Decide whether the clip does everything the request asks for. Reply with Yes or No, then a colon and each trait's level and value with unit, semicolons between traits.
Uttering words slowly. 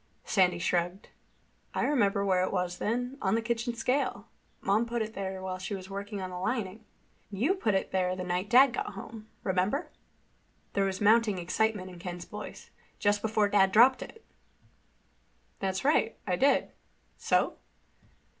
No: average, 165 wpm